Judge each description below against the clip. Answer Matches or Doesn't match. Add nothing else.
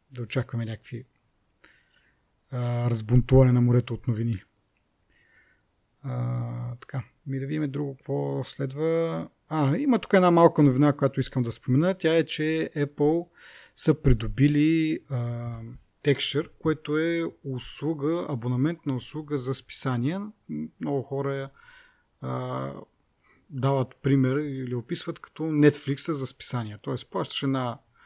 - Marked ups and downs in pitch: Doesn't match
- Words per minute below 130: Matches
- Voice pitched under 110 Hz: Doesn't match